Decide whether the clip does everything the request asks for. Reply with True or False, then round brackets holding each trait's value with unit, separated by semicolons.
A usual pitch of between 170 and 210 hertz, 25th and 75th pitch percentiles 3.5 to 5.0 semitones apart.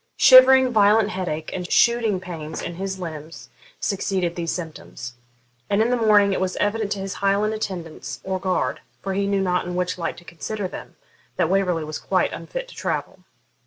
False (190 Hz; 3.1 semitones)